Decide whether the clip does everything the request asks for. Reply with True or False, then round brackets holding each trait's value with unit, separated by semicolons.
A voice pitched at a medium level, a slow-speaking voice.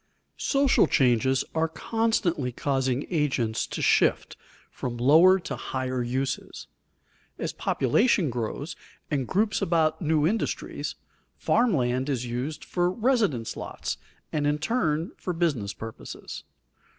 True (150 Hz; 120 wpm)